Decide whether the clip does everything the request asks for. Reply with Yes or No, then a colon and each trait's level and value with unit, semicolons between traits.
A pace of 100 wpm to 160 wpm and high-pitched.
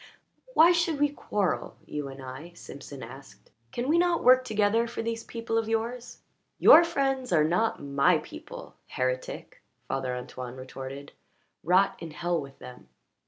Yes: average, 155 wpm; high, 210 Hz